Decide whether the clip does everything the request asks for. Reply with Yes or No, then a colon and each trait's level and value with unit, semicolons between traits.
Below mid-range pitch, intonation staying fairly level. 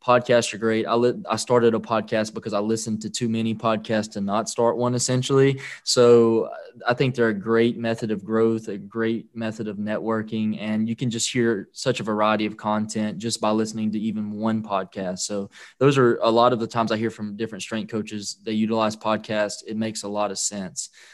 Yes: low, 110 Hz; narrow, 1.3 semitones